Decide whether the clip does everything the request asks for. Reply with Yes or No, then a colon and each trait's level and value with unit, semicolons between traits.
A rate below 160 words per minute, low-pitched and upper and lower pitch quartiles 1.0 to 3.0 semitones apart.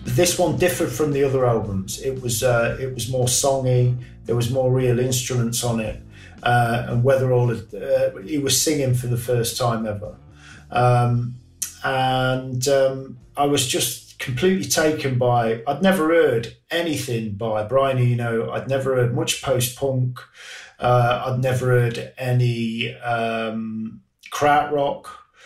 Yes: average, 150 wpm; low, 125 Hz; narrow, 2.6 semitones